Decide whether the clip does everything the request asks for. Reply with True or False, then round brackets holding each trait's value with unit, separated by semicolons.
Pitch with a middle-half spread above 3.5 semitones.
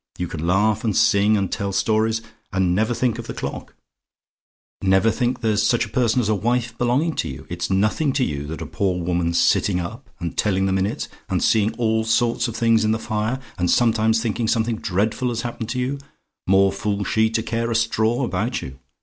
False (3.2 semitones)